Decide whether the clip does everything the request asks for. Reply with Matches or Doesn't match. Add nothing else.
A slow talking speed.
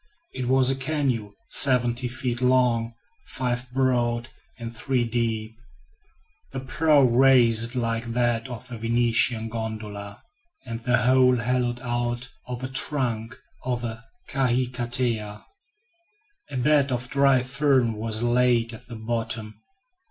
Matches